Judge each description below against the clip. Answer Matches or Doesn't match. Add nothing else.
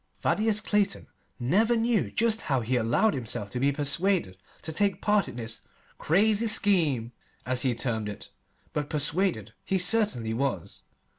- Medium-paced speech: Matches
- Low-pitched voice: Doesn't match